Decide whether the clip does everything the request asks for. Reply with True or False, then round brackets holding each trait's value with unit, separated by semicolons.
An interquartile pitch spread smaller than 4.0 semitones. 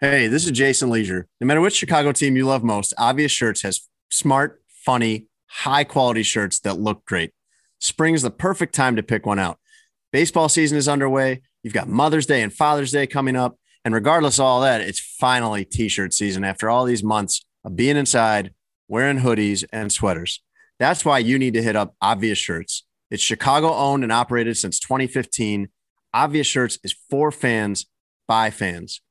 False (4.9 semitones)